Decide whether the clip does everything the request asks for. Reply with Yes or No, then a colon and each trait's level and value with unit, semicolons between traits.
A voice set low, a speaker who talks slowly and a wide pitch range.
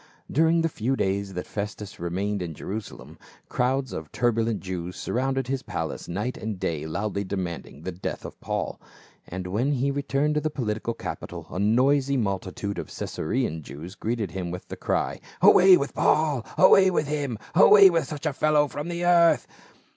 No: low, 115 Hz; average, 175 wpm; wide, 7.1 semitones